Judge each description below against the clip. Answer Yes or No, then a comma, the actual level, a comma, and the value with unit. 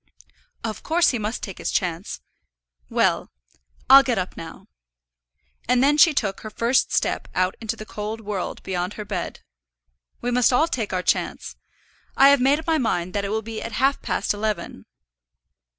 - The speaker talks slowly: No, average, 180 wpm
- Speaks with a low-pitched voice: No, high, 220 Hz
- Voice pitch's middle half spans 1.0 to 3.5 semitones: No, average, 4.6 semitones